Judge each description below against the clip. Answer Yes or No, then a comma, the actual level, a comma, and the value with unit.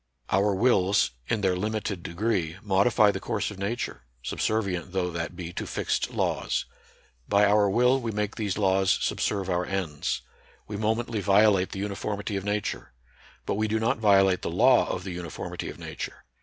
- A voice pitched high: No, low, 100 Hz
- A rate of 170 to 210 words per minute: Yes, average, 175 wpm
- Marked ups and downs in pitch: No, narrow, 2.4 semitones